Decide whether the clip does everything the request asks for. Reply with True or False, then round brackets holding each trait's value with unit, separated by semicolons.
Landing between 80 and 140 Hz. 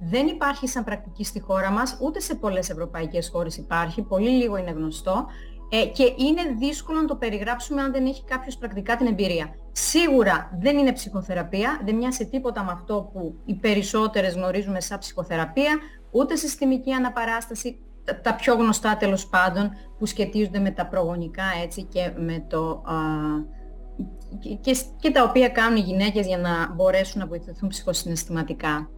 False (205 Hz)